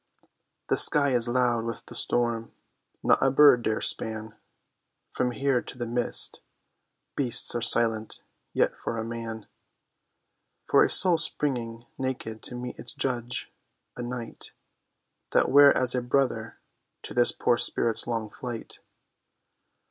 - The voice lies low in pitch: Yes, low, 120 Hz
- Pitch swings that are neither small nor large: No, narrow, 1.7 semitones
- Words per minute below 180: Yes, average, 140 wpm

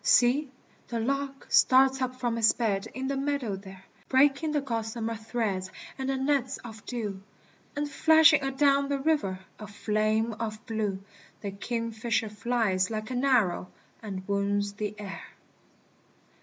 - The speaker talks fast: No, average, 150 wpm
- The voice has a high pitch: Yes, high, 230 Hz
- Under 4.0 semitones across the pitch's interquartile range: No, average, 4.4 semitones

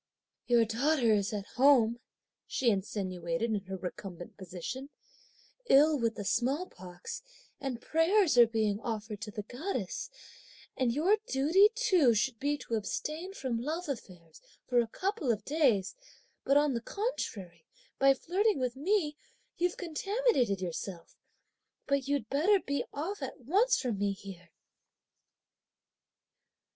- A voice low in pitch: No, very high, 250 Hz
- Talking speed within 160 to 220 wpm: No, slow, 135 wpm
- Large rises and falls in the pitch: Yes, wide, 7.3 semitones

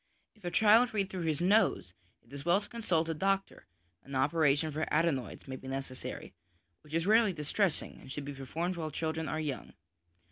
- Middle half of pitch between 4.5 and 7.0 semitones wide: Yes, average, 5.2 semitones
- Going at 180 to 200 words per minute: Yes, average, 190 wpm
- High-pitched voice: No, medium, 160 Hz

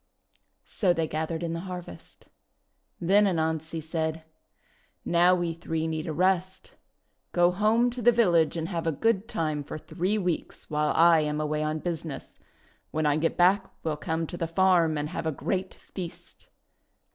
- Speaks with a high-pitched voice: No, medium, 165 Hz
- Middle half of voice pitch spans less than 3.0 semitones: Yes, narrow, 2.5 semitones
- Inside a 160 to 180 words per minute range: Yes, average, 170 wpm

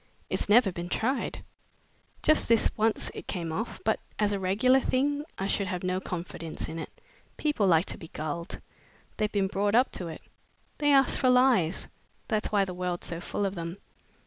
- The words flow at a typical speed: Yes, average, 190 wpm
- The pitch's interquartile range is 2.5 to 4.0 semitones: No, average, 5.0 semitones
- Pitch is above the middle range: Yes, high, 200 Hz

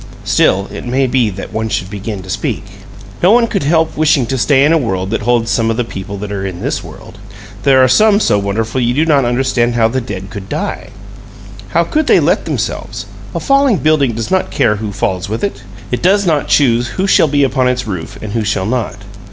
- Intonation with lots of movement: Yes, wide, 5.9 semitones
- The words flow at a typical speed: No, fast, 230 wpm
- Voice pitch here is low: Yes, low, 120 Hz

